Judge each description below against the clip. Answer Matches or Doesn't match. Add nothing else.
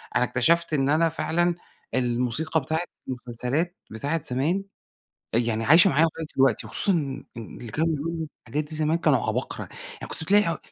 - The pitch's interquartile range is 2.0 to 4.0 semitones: Doesn't match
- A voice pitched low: Doesn't match